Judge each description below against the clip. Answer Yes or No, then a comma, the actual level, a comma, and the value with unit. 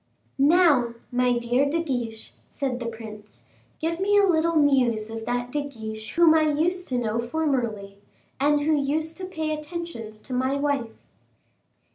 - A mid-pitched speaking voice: No, very high, 275 Hz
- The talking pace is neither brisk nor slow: Yes, average, 160 wpm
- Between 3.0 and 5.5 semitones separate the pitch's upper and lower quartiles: Yes, average, 5.2 semitones